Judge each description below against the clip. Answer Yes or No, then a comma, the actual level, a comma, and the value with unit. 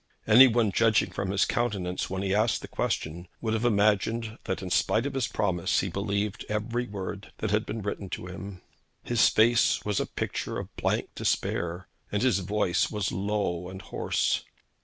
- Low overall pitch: Yes, low, 105 Hz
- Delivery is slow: No, average, 180 wpm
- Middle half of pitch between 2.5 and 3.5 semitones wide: Yes, average, 2.8 semitones